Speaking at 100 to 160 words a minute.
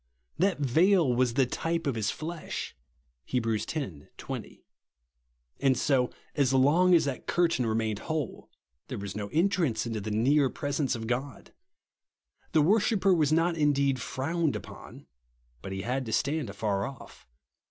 Yes: average, 145 wpm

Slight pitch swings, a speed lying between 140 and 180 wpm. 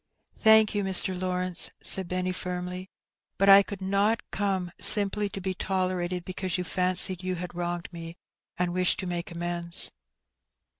Yes: narrow, 1.5 semitones; average, 170 wpm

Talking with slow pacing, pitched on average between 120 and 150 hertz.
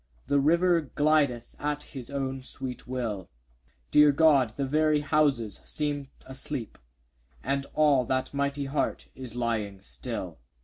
Yes: slow, 130 wpm; medium, 140 Hz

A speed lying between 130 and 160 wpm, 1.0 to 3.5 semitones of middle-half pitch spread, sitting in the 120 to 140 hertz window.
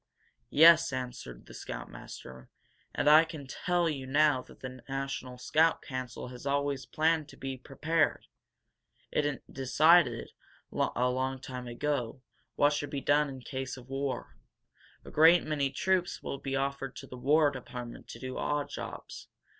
Yes: average, 155 wpm; average, 2.7 semitones; low, 135 Hz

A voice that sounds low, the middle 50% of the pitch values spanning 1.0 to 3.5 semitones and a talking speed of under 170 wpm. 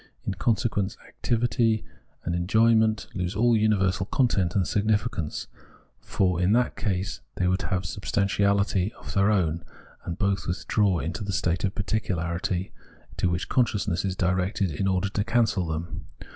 Yes: low, 100 Hz; average, 3.1 semitones; average, 155 wpm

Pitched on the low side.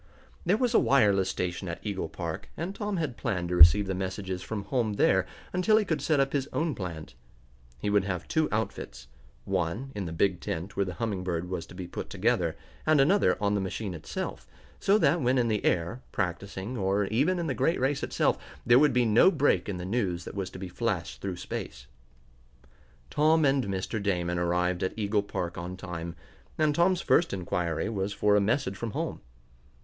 Yes: low, 100 Hz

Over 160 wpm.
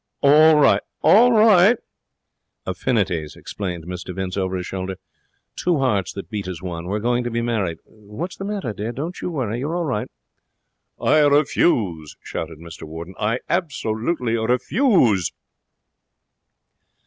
No: average, 140 wpm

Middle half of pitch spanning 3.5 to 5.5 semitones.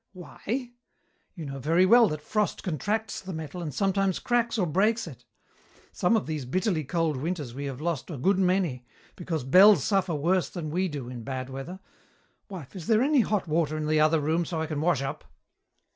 Yes: average, 4.4 semitones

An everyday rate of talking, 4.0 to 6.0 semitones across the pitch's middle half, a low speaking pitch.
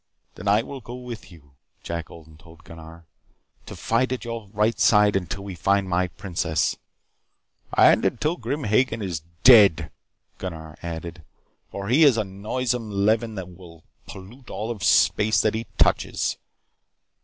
Yes: average, 155 wpm; average, 5.2 semitones; low, 100 Hz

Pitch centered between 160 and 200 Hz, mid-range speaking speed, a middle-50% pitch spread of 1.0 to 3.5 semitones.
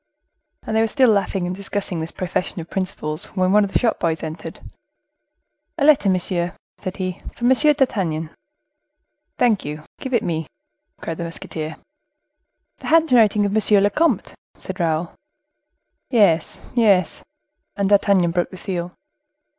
No: high, 190 Hz; average, 150 wpm; average, 4.3 semitones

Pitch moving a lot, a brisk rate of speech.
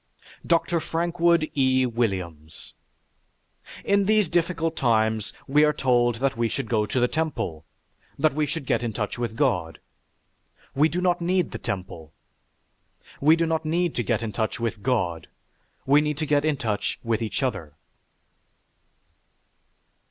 No: wide, 6.4 semitones; average, 150 wpm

